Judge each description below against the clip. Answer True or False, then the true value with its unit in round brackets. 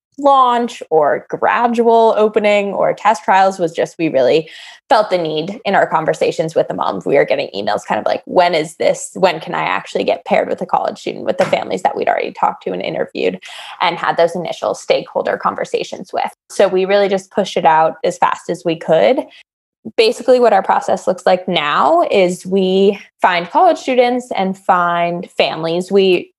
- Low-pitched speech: False (195 Hz)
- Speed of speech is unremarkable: True (195 wpm)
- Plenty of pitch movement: True (6.1 semitones)